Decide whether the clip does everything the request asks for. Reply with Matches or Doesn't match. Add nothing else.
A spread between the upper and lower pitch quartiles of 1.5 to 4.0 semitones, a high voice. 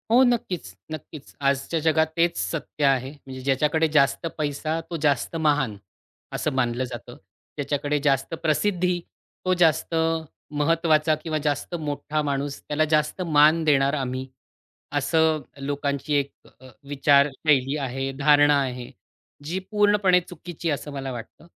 Doesn't match